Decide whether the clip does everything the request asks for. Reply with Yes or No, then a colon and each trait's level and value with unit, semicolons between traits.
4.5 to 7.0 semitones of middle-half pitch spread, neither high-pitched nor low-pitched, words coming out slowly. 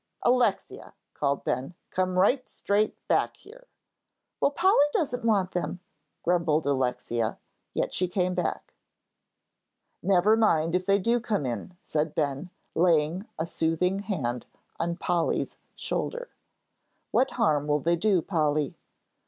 Yes: average, 5.3 semitones; medium, 180 Hz; slow, 130 wpm